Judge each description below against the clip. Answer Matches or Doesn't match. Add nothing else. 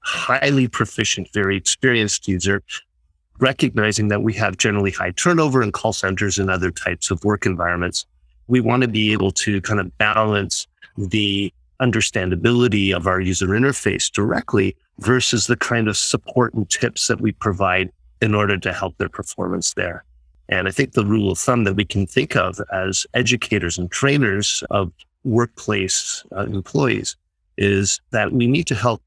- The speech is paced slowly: Doesn't match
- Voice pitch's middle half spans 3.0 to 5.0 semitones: Matches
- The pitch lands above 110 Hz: Doesn't match